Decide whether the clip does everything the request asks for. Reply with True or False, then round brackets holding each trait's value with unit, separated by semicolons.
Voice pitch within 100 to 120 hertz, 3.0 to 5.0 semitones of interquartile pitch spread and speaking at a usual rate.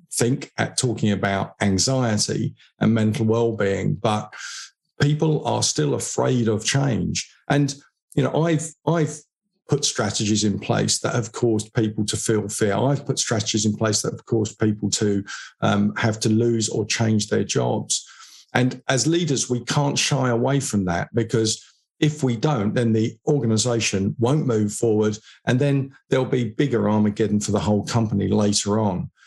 True (115 Hz; 4.0 semitones; 165 wpm)